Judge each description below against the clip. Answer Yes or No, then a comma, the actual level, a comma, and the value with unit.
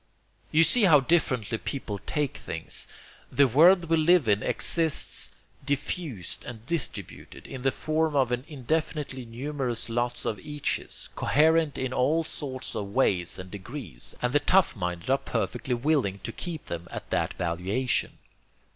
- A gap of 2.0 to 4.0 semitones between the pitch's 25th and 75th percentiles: No, wide, 5.4 semitones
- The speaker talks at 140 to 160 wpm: Yes, average, 150 wpm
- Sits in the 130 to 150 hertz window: Yes, low, 135 Hz